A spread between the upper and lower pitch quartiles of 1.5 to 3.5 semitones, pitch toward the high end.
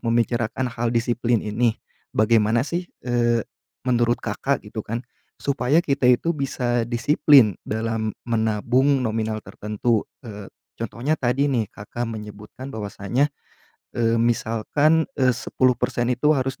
No: average, 2.7 semitones; low, 120 Hz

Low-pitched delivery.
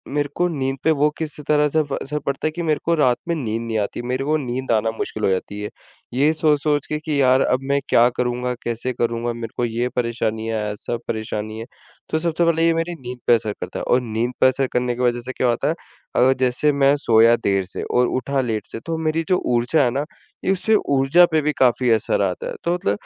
Yes: low, 130 Hz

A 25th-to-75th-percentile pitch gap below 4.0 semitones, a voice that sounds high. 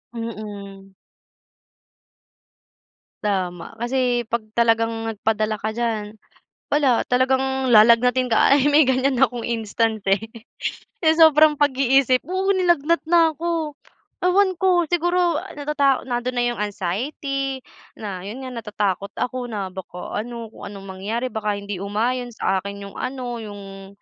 No: average, 4.6 semitones; high, 240 Hz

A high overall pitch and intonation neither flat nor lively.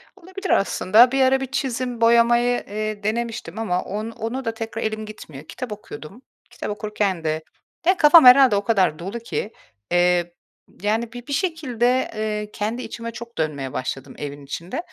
Yes: high, 220 Hz; average, 3.9 semitones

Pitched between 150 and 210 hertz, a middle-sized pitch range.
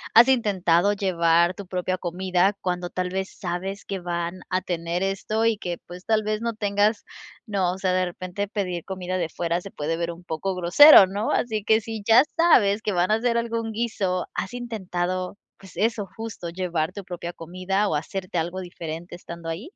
Yes: medium, 185 Hz; average, 3.1 semitones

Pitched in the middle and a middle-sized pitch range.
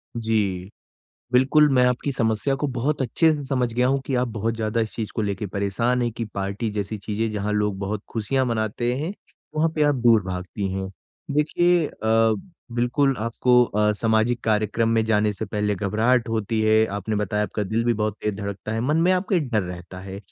No: low, 110 Hz; average, 3.2 semitones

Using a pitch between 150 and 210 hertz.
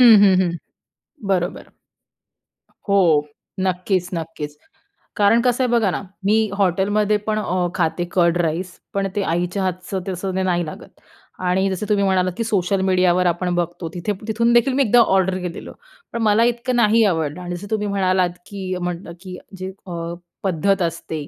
Yes: high, 190 Hz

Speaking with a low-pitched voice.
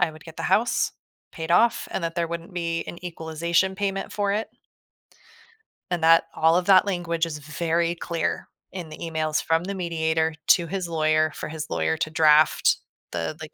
No: medium, 165 Hz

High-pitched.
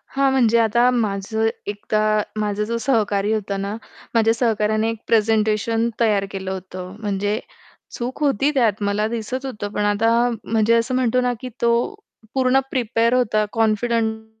Yes: high, 220 Hz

